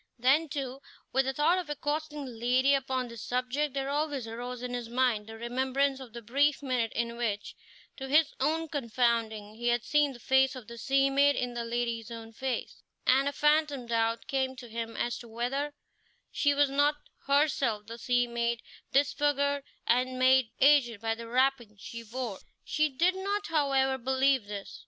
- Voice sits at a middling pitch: No, very high, 260 Hz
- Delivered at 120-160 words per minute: No, average, 185 wpm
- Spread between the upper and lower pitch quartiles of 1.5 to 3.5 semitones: Yes, average, 3.2 semitones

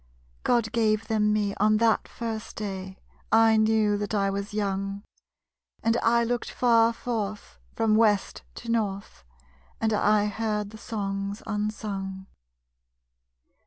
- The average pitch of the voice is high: Yes, high, 215 Hz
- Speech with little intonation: Yes, narrow, 1.9 semitones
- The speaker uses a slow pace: Yes, slow, 125 wpm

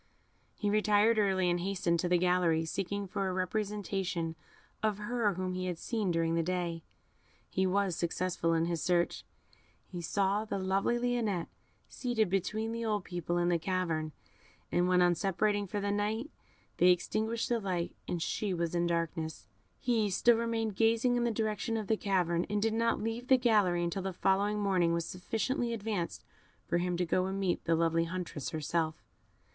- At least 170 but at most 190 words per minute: Yes, average, 180 wpm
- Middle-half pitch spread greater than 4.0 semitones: No, average, 3.6 semitones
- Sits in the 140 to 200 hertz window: Yes, high, 190 Hz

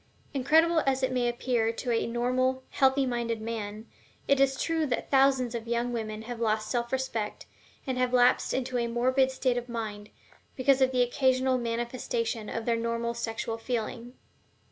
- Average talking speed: Yes, average, 170 wpm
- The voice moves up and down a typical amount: No, narrow, 2.1 semitones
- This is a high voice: Yes, high, 245 Hz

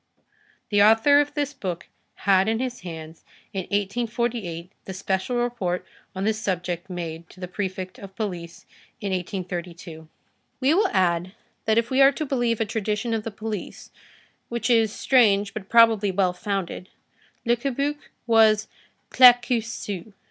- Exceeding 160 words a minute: No, average, 150 wpm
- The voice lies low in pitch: No, high, 210 Hz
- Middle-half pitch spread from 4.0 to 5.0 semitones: Yes, average, 4.3 semitones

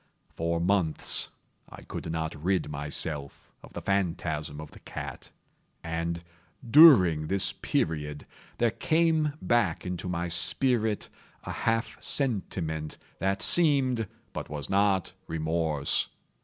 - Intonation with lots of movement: Yes, wide, 5.9 semitones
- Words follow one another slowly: Yes, slow, 115 wpm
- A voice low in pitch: Yes, very low, 85 Hz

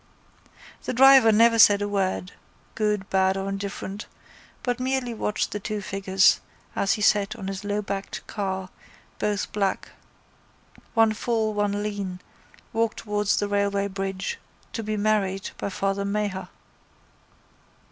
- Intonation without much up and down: Yes, narrow, 1.7 semitones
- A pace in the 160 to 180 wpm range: No, slow, 135 wpm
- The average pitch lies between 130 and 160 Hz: No, high, 205 Hz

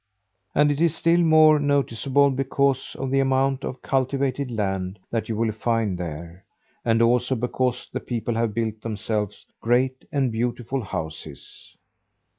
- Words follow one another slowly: No, average, 145 wpm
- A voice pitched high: No, low, 125 Hz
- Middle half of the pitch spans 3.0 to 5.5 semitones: Yes, average, 3.7 semitones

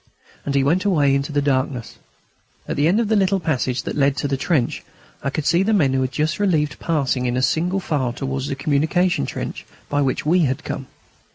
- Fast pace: Yes, fast, 225 wpm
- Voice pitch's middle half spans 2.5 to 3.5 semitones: No, average, 4.1 semitones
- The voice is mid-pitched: Yes, medium, 145 Hz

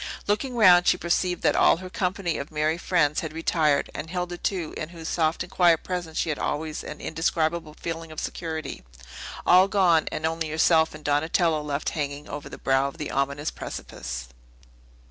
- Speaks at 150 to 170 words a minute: No, average, 185 wpm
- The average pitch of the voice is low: No, medium, 160 Hz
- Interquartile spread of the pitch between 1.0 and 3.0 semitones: Yes, narrow, 2.6 semitones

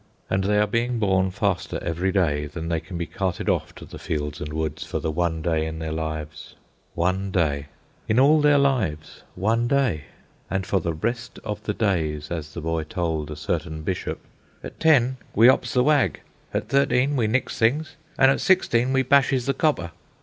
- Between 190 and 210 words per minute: Yes, average, 195 wpm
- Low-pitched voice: Yes, very low, 95 Hz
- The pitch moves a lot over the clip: Yes, wide, 7.6 semitones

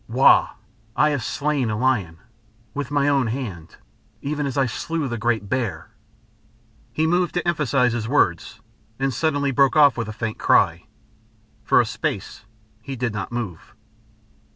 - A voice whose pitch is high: No, low, 130 Hz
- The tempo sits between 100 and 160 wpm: Yes, average, 155 wpm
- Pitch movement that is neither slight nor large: Yes, average, 4.3 semitones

